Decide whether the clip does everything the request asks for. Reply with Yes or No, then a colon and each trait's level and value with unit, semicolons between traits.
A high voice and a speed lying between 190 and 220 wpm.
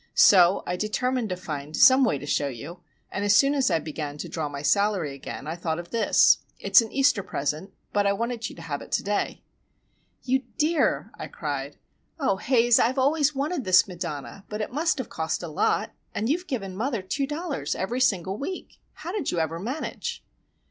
Yes: high, 205 Hz; average, 200 wpm